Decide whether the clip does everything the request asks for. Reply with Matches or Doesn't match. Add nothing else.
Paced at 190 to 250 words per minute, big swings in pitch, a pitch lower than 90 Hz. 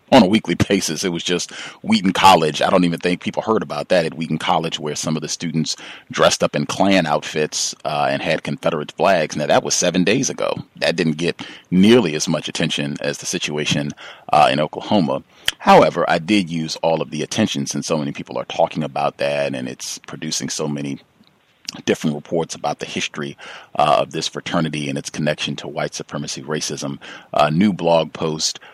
Doesn't match